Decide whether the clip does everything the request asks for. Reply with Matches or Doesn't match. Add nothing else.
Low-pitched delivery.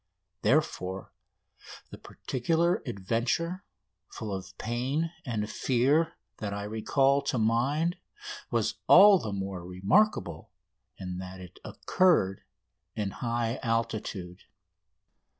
Matches